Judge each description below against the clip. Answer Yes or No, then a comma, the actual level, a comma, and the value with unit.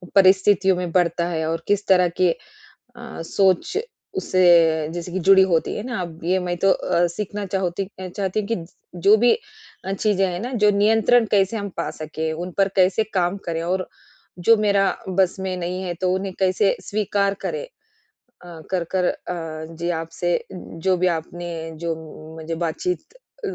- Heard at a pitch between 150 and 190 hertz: Yes, medium, 185 Hz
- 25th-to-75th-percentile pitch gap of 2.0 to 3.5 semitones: Yes, narrow, 2.5 semitones